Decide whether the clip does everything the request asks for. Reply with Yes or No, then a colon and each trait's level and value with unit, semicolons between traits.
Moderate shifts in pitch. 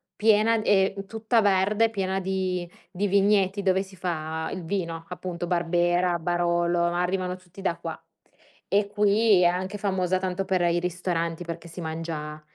No: narrow, 2.3 semitones